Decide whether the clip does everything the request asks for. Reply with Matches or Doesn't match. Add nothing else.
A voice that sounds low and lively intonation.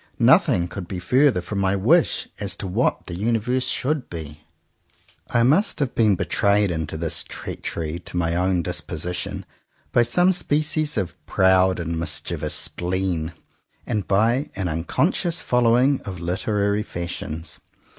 Matches